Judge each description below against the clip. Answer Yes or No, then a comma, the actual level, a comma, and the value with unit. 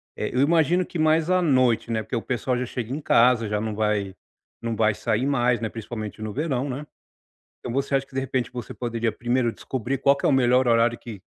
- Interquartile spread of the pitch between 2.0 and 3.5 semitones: Yes, average, 3.1 semitones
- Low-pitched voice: Yes, low, 125 Hz